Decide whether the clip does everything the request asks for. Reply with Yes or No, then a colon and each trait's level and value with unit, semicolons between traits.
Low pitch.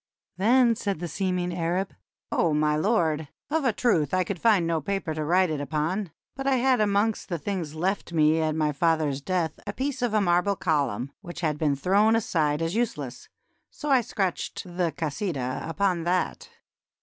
No: medium, 175 Hz